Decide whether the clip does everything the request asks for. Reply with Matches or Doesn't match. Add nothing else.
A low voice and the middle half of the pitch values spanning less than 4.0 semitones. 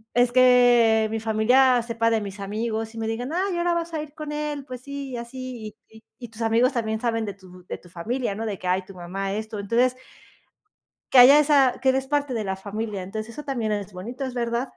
Doesn't match